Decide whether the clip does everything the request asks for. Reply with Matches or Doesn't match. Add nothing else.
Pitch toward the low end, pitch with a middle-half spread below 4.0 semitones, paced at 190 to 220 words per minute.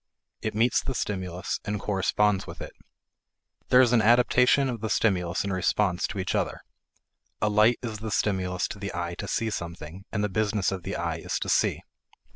Matches